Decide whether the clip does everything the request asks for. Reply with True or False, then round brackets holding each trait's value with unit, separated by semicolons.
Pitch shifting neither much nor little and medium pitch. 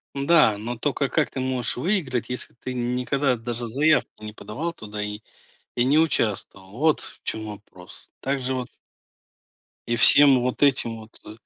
False (3.9 semitones; 125 Hz)